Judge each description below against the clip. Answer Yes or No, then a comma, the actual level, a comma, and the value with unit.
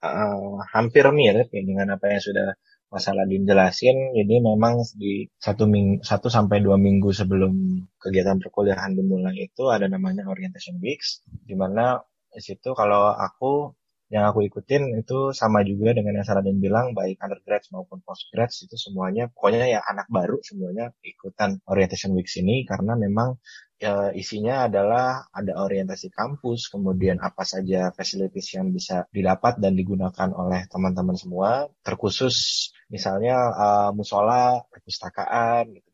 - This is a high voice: No, low, 100 Hz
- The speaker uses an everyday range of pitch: Yes, average, 3.6 semitones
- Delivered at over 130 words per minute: Yes, fast, 140 wpm